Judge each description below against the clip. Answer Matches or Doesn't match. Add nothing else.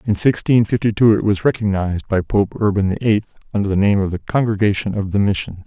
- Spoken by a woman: Doesn't match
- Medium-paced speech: Doesn't match